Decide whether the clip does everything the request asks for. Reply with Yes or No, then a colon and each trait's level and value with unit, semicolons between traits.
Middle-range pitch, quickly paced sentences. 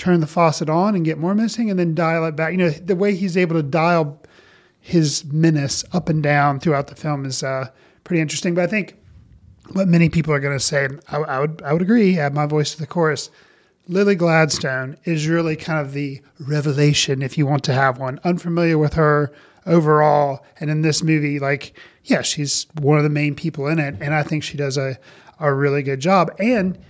Yes: medium, 155 Hz; fast, 220 wpm